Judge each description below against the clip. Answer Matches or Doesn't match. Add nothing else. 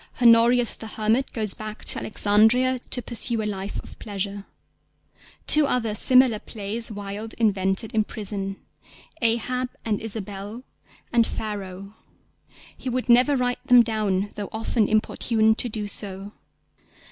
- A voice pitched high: Matches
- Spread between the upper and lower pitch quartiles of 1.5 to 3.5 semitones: Matches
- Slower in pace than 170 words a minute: Matches